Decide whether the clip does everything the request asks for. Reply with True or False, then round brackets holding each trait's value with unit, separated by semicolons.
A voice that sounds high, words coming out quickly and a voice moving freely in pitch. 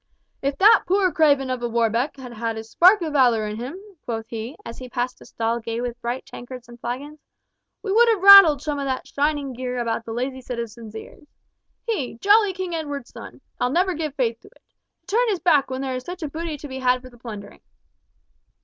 False (260 Hz; 220 wpm; 4.9 semitones)